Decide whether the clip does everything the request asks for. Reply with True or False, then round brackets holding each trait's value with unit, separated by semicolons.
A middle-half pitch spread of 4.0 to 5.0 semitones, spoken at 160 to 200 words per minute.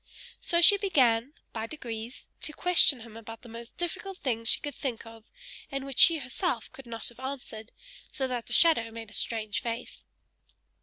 True (4.5 semitones; 185 wpm)